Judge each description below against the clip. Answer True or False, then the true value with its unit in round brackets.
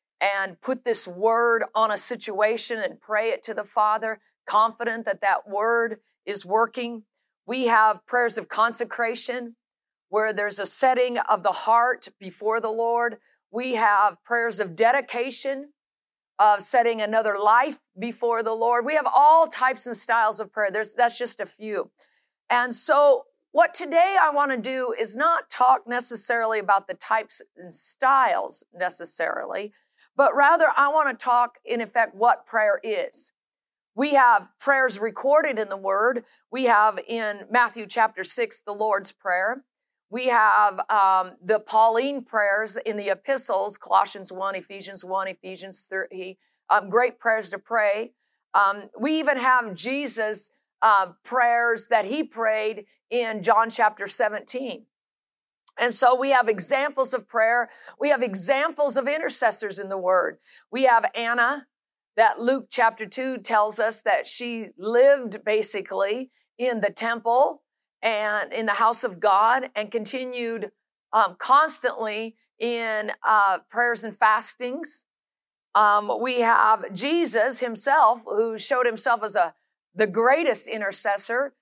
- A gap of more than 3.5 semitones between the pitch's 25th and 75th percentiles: False (2.9 semitones)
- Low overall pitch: False (230 Hz)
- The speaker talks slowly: False (145 wpm)